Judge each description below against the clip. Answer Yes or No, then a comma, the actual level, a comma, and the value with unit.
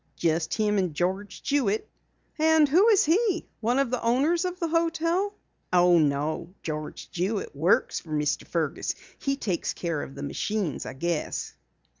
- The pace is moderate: Yes, average, 160 wpm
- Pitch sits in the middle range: No, high, 205 Hz